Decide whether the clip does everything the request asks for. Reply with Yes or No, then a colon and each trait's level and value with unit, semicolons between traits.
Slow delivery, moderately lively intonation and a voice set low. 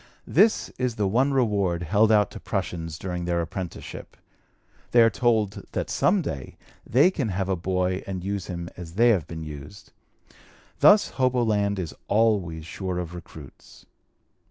No: average, 155 wpm; average, 4.6 semitones; very low, 95 Hz